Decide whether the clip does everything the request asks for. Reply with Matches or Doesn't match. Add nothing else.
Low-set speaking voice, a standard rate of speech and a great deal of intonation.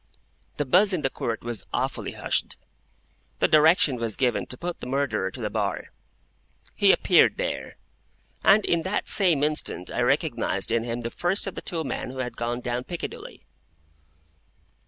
Matches